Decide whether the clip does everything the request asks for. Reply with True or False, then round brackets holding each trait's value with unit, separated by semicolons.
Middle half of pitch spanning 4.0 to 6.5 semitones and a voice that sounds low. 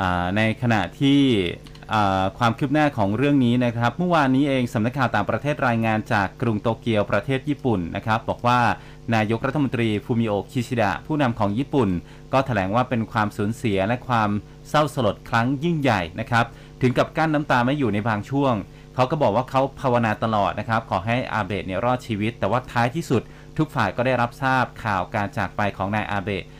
True (4.3 semitones; 120 Hz)